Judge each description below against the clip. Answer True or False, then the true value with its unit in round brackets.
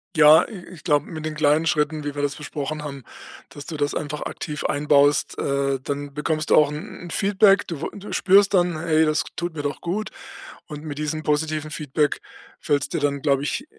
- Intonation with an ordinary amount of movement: False (1.8 semitones)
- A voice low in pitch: False (150 Hz)